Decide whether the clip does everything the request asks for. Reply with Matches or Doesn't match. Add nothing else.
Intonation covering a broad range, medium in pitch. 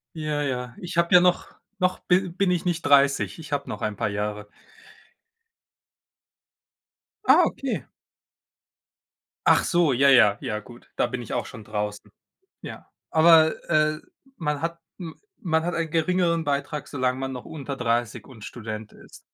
Matches